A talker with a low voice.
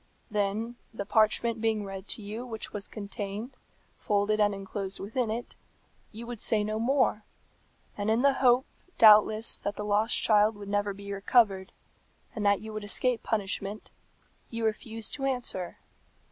No: high, 215 Hz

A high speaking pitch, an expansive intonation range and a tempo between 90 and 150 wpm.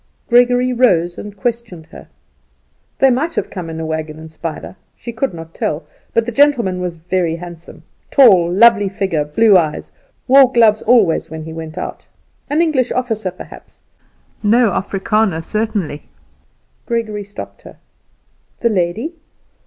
Yes: high, 205 Hz; wide, 6.0 semitones; average, 145 wpm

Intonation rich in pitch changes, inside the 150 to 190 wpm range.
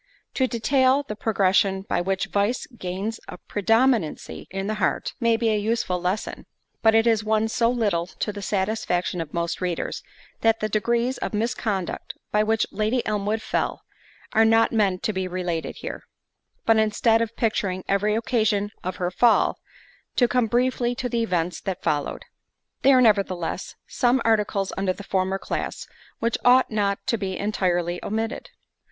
No: average, 3.3 semitones; average, 165 wpm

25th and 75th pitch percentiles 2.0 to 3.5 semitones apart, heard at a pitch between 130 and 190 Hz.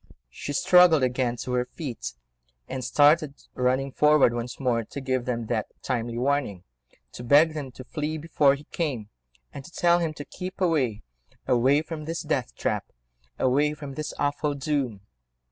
No: average, 3.9 semitones; low, 135 Hz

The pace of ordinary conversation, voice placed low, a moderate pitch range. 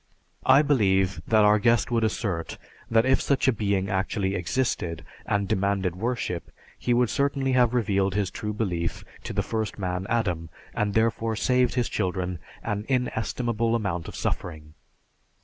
Yes: average, 155 wpm; low, 105 Hz; average, 3.9 semitones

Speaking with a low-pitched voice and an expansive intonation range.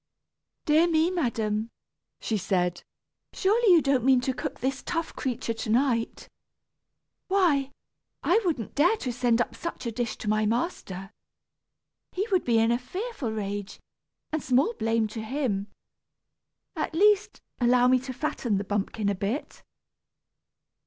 No: very high, 250 Hz; wide, 6.3 semitones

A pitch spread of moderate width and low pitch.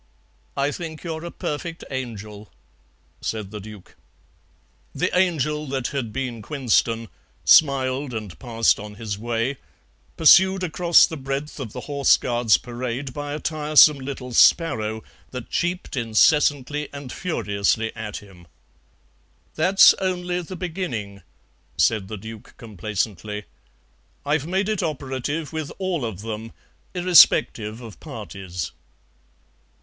No: wide, 6.1 semitones; low, 130 Hz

